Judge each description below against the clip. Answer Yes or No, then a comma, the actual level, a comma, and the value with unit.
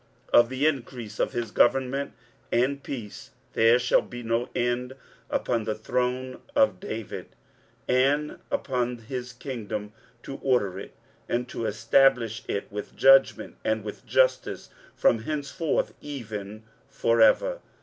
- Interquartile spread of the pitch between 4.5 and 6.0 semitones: No, average, 3.3 semitones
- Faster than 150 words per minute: No, slow, 135 wpm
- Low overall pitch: Yes, low, 125 Hz